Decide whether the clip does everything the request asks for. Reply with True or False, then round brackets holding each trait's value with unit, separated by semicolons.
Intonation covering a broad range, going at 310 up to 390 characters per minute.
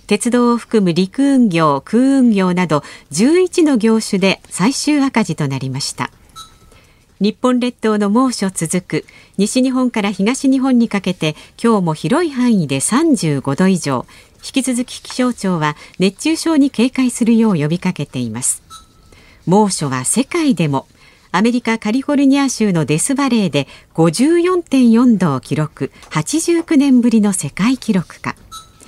False (7.6 semitones; 260 characters per minute)